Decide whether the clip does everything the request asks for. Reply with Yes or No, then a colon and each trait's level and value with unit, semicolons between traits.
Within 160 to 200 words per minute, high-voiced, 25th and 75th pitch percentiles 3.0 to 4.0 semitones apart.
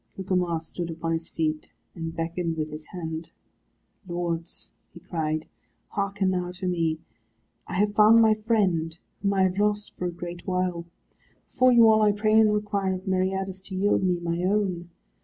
No: average, 175 wpm; medium, 180 Hz; average, 3.3 semitones